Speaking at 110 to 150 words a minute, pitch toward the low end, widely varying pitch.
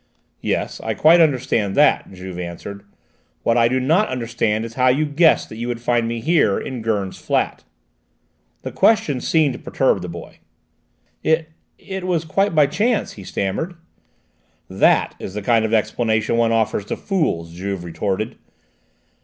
No: average, 160 wpm; low, 115 Hz; wide, 6.9 semitones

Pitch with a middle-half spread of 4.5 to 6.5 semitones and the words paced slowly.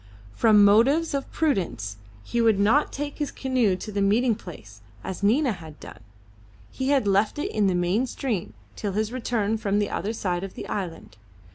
No: average, 4.8 semitones; average, 185 wpm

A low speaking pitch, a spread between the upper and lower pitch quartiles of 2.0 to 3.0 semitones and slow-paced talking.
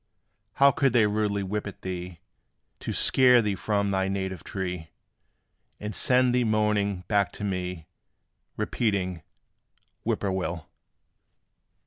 Yes: low, 100 Hz; narrow, 2.6 semitones; slow, 125 wpm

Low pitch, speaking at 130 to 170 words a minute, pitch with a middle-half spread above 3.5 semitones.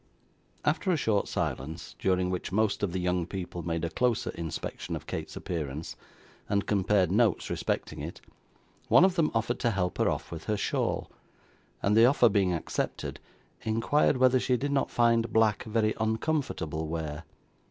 Yes: low, 105 Hz; average, 165 wpm; average, 5.0 semitones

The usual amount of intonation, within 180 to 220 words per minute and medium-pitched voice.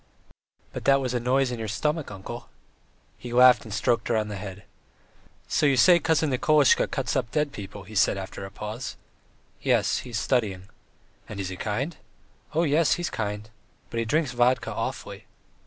No: average, 4.9 semitones; average, 185 wpm; low, 120 Hz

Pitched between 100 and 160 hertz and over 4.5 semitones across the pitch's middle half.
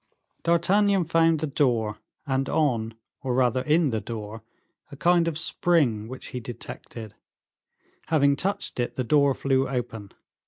Yes: low, 135 Hz; wide, 5.5 semitones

